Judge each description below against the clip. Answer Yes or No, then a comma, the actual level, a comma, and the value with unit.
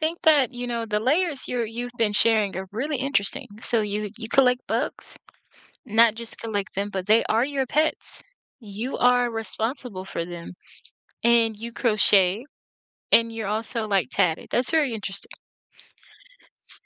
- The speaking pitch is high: Yes, high, 230 Hz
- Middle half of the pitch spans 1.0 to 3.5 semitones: Yes, average, 3.1 semitones